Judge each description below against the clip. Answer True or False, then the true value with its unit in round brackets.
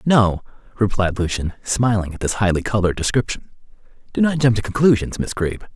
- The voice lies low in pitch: True (105 Hz)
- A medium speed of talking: True (165 wpm)